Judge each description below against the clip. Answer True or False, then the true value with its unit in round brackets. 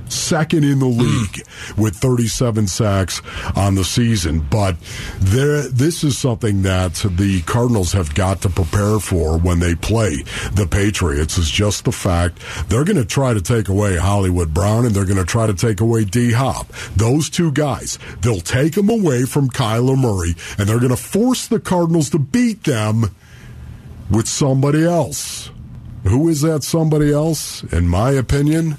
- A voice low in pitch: True (115 Hz)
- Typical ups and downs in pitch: False (6.0 semitones)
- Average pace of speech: True (170 wpm)